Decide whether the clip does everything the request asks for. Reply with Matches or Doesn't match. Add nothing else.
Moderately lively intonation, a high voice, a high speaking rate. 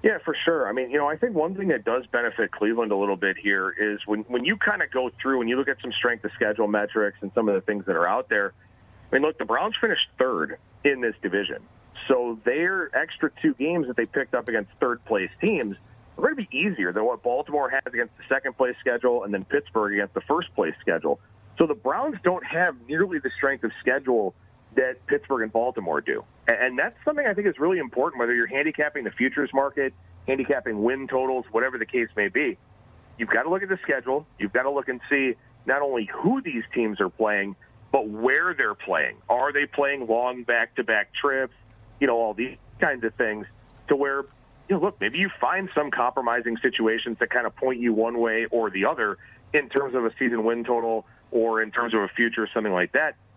Doesn't match